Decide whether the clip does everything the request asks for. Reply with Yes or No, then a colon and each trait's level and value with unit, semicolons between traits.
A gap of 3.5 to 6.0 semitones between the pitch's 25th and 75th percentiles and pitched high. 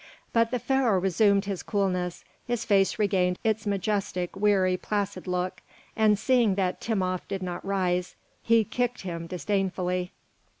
No: average, 2.9 semitones; high, 195 Hz